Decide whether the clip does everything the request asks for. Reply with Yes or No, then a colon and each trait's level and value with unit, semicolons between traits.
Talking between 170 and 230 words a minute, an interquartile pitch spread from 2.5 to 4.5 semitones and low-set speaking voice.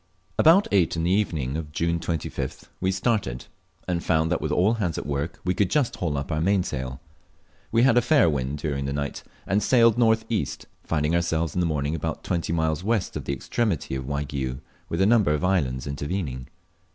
No: average, 200 wpm; wide, 5.5 semitones; very low, 85 Hz